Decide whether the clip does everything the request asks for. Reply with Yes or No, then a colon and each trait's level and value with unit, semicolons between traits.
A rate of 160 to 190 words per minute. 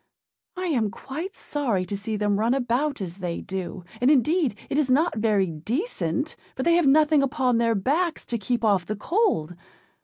Yes: average, 185 wpm